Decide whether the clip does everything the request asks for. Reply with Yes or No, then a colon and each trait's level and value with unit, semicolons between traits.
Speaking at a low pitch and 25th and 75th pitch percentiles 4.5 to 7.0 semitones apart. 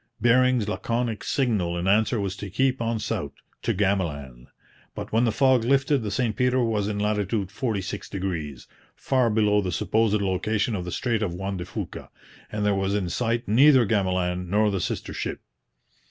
No: low, 105 Hz; average, 3.5 semitones